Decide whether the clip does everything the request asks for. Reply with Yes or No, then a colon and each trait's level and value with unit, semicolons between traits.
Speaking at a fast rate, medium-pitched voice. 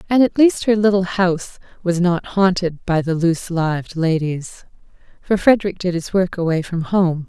No: average, 180 wpm; medium, 180 Hz